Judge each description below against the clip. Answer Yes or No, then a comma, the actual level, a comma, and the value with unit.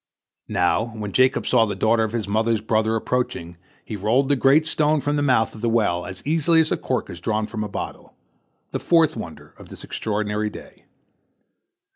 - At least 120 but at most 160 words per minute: No, average, 190 wpm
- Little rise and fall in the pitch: No, average, 4.2 semitones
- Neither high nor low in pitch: No, low, 110 Hz